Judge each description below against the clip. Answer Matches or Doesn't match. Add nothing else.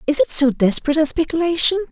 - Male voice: Doesn't match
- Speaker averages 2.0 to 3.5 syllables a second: Doesn't match